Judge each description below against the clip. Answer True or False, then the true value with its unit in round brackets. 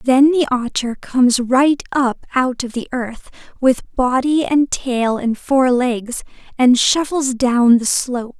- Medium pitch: False (255 Hz)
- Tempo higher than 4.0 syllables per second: False (3.7 syllables/s)